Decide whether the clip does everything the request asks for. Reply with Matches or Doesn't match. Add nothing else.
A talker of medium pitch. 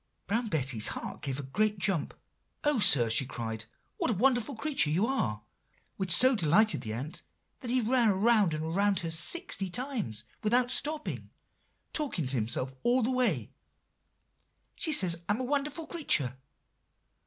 Doesn't match